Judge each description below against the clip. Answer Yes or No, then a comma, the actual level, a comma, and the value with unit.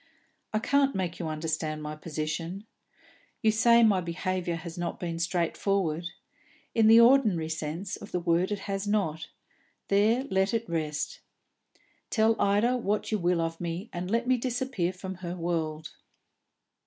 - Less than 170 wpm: Yes, average, 155 wpm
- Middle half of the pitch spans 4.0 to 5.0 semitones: Yes, average, 4.5 semitones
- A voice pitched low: No, medium, 185 Hz